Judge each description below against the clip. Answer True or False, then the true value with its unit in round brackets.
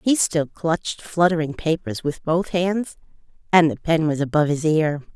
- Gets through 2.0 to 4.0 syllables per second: False (4.8 syllables/s)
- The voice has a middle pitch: True (160 Hz)